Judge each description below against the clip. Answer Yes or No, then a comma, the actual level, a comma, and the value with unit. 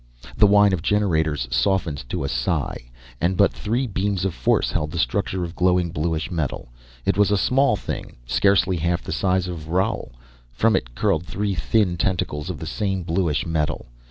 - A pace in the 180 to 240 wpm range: Yes, average, 185 wpm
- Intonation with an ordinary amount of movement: Yes, average, 3.9 semitones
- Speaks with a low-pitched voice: Yes, very low, 90 Hz